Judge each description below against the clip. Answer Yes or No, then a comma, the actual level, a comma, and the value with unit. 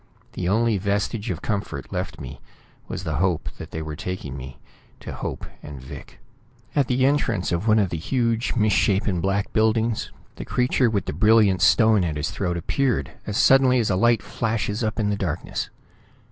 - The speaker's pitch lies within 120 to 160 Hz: No, low, 105 Hz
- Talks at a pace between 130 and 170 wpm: No, average, 185 wpm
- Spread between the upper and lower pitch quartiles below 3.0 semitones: No, average, 4.6 semitones